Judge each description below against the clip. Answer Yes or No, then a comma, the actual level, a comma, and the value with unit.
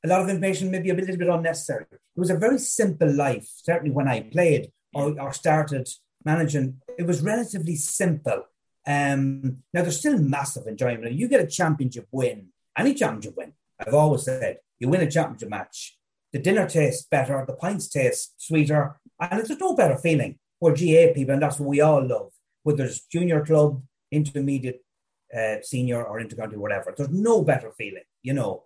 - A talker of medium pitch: Yes, medium, 150 Hz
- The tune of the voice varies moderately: Yes, average, 4.4 semitones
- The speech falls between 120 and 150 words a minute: No, average, 185 wpm